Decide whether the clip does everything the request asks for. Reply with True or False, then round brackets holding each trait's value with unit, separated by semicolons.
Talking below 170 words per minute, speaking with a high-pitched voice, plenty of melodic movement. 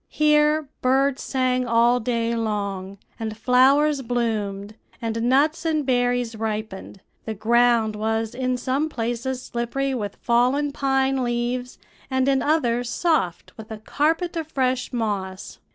False (135 wpm; 245 Hz; 3.3 semitones)